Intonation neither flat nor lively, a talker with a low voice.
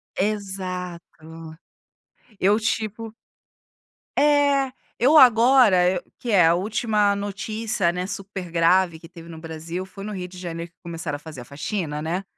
No: average, 4.2 semitones; medium, 185 Hz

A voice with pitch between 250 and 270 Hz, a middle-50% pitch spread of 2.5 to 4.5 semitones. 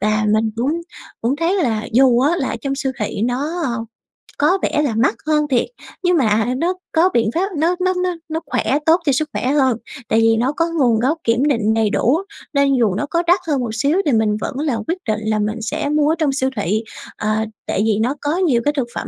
No: very high, 265 Hz; average, 5.3 semitones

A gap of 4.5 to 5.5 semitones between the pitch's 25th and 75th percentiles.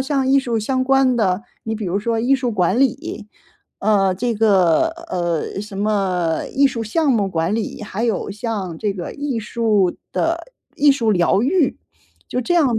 Yes: average, 4.9 semitones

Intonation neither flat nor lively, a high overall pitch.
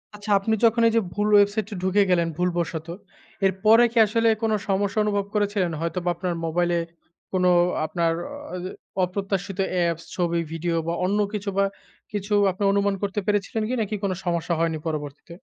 Yes: average, 3.1 semitones; high, 195 Hz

